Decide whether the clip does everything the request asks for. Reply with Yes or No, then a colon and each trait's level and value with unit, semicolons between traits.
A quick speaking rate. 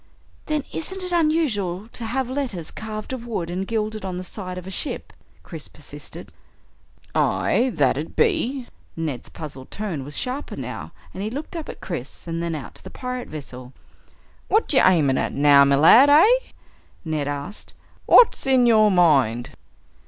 No: average, 170 wpm